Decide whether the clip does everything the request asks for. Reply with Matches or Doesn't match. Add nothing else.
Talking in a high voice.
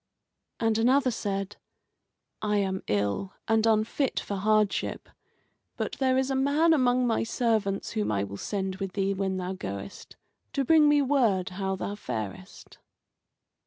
Matches